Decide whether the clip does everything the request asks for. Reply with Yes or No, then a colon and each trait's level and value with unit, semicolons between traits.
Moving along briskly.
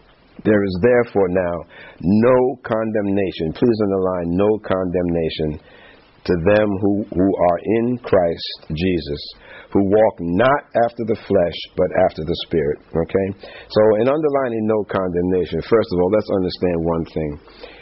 No: average, 140 wpm